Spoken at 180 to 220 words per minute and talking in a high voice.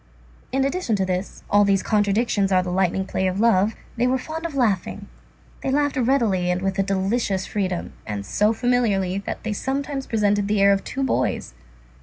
Yes: average, 185 wpm; high, 205 Hz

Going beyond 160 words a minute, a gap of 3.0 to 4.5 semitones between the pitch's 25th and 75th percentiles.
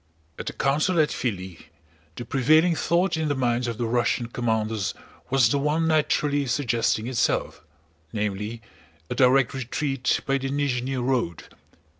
No: average, 145 wpm; average, 3.6 semitones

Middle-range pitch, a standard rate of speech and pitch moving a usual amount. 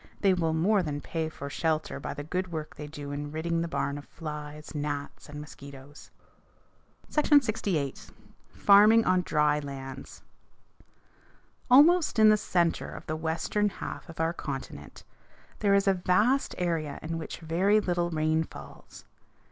Yes: medium, 160 Hz; average, 155 wpm; average, 4.2 semitones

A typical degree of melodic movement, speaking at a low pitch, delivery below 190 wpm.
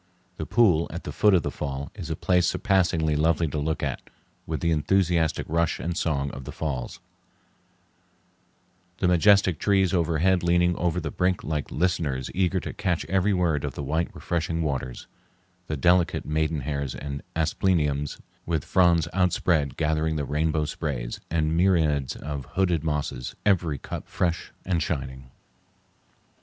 Yes: average, 3.1 semitones; very low, 80 Hz; average, 155 wpm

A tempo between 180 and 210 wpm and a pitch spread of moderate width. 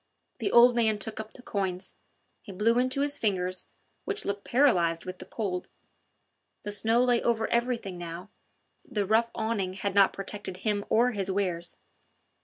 No: average, 165 wpm; average, 3.9 semitones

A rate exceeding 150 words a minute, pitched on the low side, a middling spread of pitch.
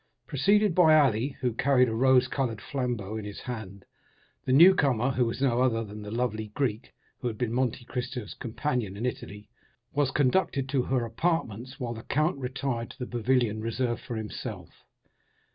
Yes: average, 180 wpm; low, 125 Hz; average, 3.2 semitones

